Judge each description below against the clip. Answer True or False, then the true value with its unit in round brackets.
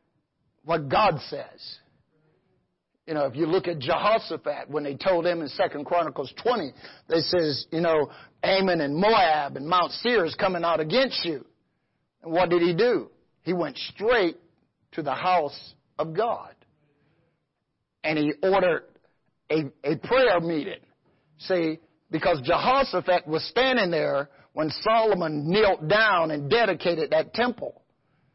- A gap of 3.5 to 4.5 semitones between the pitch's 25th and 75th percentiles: True (4.0 semitones)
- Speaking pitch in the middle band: True (165 Hz)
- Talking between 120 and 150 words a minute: True (140 wpm)